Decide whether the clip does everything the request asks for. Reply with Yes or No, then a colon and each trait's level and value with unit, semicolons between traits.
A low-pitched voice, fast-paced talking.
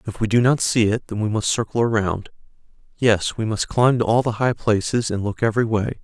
Yes: low, 110 Hz; fast, 240 wpm